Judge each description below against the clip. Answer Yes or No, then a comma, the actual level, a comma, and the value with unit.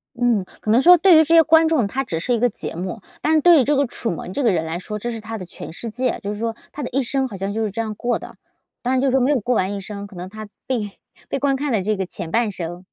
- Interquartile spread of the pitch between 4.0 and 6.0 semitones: Yes, average, 5.0 semitones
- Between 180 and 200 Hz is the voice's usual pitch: No, high, 230 Hz